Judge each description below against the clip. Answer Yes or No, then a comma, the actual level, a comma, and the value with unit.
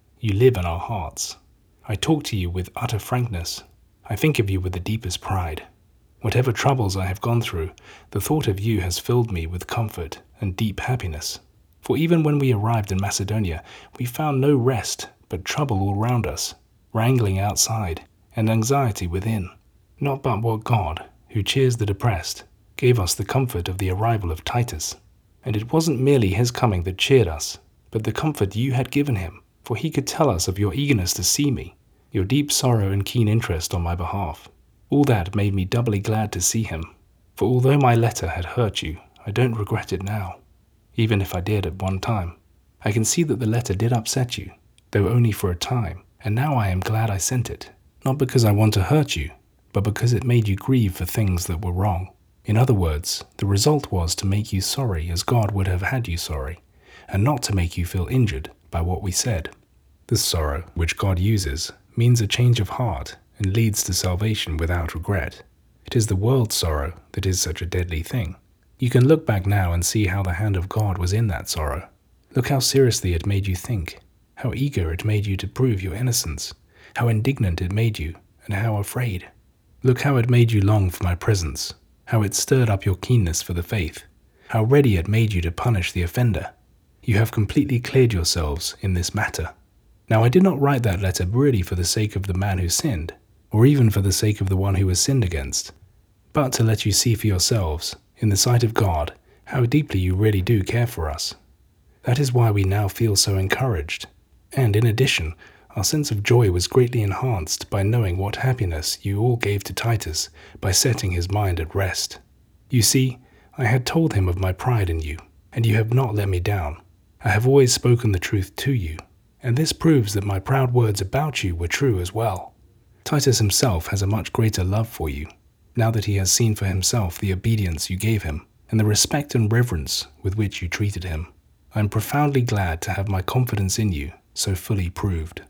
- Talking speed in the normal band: No, fast, 210 wpm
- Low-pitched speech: Yes, low, 105 Hz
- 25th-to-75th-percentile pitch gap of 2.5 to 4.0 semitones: No, average, 4.6 semitones